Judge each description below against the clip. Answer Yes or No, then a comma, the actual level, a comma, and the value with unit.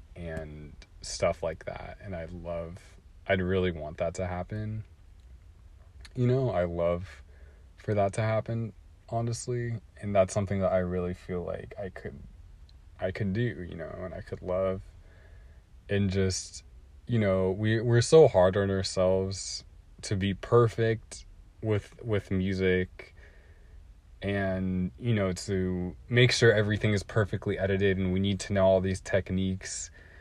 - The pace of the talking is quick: No, average, 150 wpm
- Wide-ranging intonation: No, average, 2.9 semitones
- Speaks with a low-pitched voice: Yes, very low, 95 Hz